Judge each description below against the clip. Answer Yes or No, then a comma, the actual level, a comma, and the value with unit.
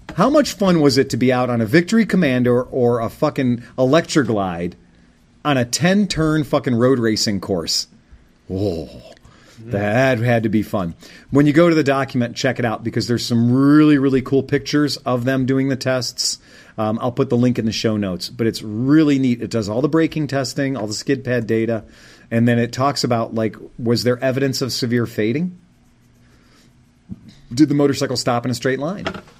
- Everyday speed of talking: Yes, average, 195 wpm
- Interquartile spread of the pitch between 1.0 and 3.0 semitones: No, average, 3.7 semitones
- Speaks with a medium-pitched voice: No, low, 125 Hz